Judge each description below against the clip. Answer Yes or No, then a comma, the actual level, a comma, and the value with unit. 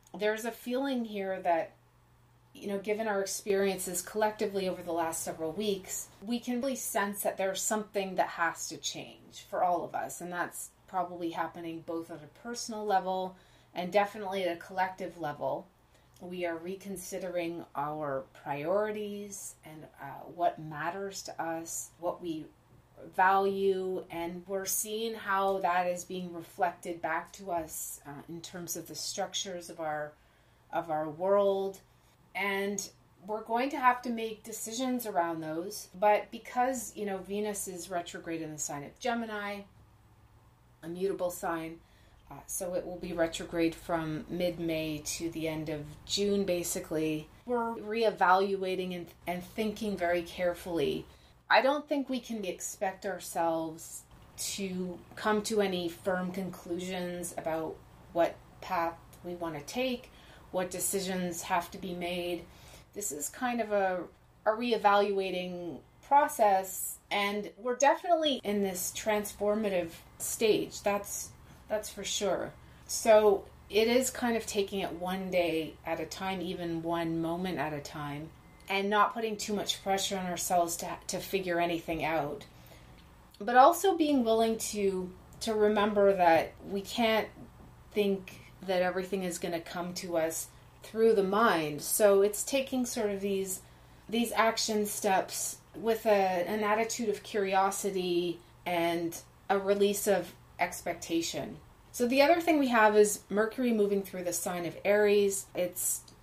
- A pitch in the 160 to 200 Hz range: Yes, medium, 185 Hz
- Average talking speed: Yes, average, 150 wpm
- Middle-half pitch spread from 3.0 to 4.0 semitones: Yes, average, 3.7 semitones